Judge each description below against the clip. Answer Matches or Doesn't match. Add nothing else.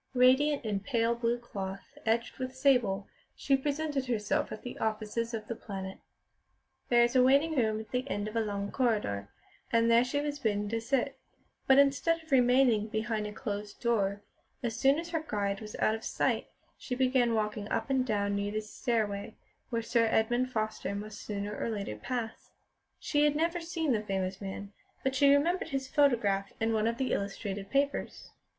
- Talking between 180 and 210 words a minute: Matches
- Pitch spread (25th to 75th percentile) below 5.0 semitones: Matches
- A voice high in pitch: Matches